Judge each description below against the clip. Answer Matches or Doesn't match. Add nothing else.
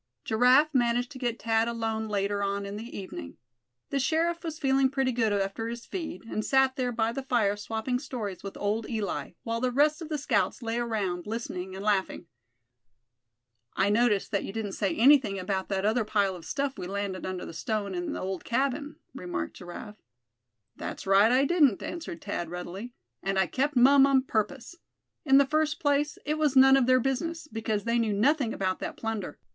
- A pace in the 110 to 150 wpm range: Doesn't match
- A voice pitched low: Doesn't match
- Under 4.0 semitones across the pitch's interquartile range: Doesn't match